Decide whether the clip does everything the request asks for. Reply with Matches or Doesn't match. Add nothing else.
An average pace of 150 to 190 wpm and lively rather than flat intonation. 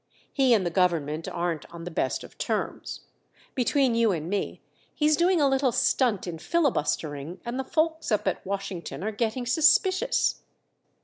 Matches